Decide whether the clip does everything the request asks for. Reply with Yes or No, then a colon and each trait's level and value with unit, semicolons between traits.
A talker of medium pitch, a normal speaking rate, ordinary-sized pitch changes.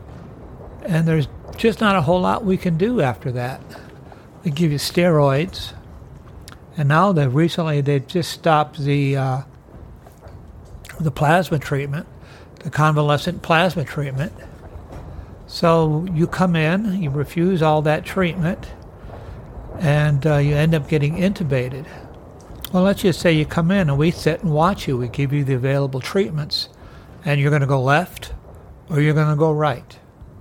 Yes: medium, 150 Hz; average, 155 wpm; average, 3.9 semitones